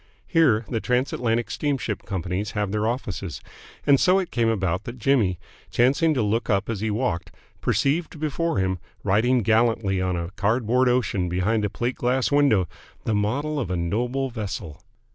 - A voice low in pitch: Yes, low, 115 Hz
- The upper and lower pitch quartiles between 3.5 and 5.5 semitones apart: Yes, average, 4.7 semitones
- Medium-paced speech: Yes, average, 170 wpm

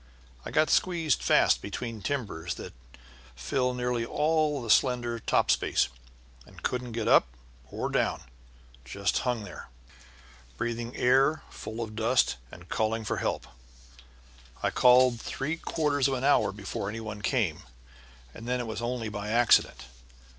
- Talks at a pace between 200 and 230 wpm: No, average, 150 wpm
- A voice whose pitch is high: No, low, 120 Hz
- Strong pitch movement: No, average, 3.1 semitones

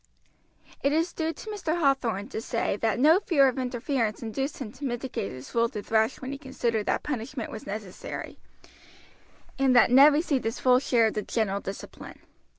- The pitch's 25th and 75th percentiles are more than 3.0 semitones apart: Yes, average, 4.1 semitones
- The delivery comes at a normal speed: Yes, average, 185 wpm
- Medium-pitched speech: No, very high, 250 Hz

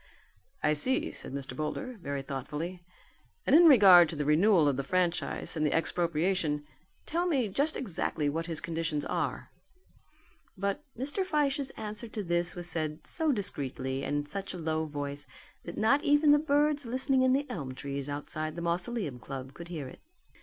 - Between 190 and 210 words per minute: No, average, 175 wpm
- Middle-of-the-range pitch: Yes, medium, 170 Hz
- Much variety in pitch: Yes, wide, 9.0 semitones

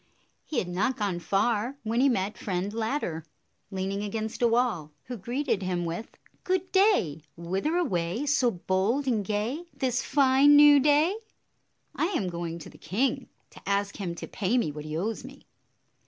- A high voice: Yes, high, 215 Hz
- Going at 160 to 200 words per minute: Yes, average, 185 wpm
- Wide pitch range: Yes, wide, 6.5 semitones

